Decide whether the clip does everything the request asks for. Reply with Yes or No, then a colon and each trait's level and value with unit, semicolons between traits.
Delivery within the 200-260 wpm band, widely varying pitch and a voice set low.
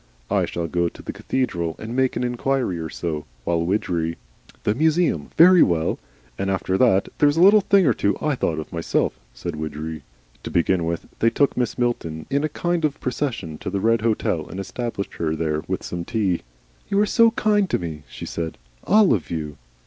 Yes: fast, 205 wpm; wide, 9.0 semitones; low, 100 Hz